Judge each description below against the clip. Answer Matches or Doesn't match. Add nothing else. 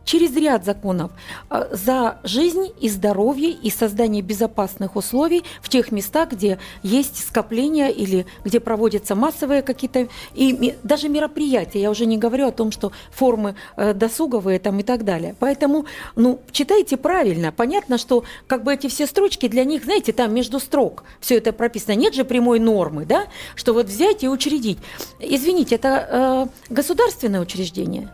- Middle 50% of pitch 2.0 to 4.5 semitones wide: Doesn't match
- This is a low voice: Doesn't match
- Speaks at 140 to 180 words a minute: Matches